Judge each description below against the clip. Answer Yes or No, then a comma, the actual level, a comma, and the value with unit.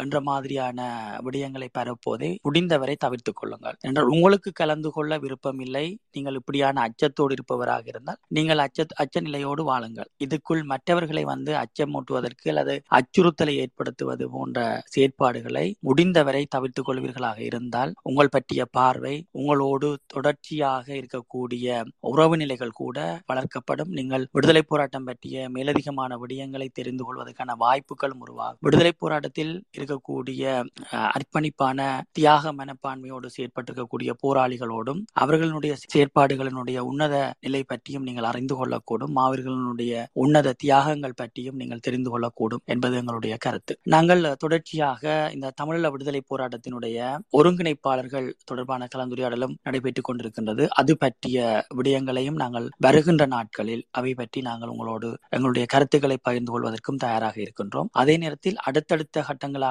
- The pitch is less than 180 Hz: Yes, low, 135 Hz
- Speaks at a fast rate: No, average, 105 wpm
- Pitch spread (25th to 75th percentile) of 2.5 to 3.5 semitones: Yes, average, 2.8 semitones